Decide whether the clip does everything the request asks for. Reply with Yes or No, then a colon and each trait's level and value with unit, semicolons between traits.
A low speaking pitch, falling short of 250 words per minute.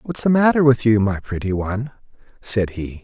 Yes: low, 115 Hz; average, 200 wpm